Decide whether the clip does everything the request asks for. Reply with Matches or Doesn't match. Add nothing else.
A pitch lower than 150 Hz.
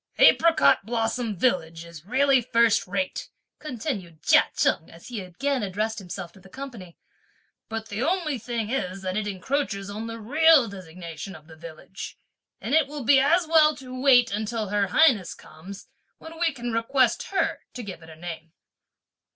Doesn't match